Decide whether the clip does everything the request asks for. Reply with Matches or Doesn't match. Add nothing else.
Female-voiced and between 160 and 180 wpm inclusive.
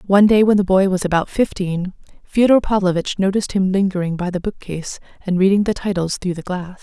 Doesn't match